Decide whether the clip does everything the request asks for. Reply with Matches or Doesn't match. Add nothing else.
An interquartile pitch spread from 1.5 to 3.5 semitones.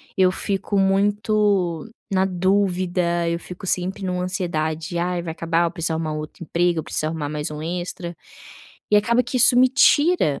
Matches